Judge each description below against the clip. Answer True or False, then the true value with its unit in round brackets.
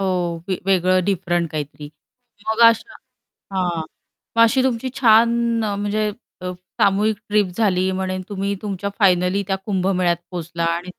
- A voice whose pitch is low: False (190 Hz)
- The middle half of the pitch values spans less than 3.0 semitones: True (2.6 semitones)